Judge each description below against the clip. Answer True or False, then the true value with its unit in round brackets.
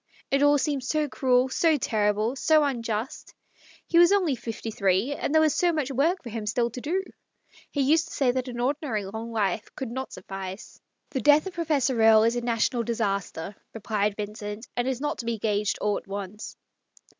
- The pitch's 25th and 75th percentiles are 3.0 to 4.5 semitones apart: False (5.3 semitones)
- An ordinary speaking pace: False (215 wpm)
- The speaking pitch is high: True (240 Hz)